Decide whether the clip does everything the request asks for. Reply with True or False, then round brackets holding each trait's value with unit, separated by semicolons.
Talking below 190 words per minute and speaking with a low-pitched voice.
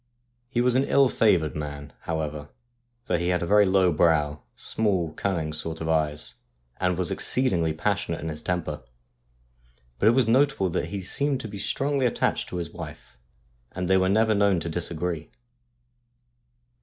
True (165 wpm; 90 Hz)